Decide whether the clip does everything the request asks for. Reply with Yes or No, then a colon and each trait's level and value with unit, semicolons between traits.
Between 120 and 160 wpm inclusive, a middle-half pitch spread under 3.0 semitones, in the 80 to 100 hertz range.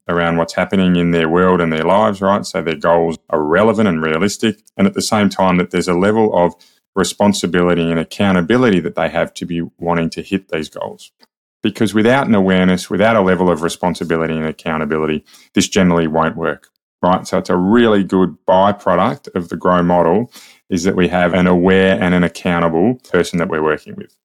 No: average, 200 wpm; narrow, 2.4 semitones; very low, 90 Hz